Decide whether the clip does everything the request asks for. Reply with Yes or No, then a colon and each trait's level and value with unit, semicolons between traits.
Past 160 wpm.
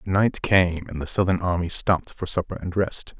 Yes: fast, 205 wpm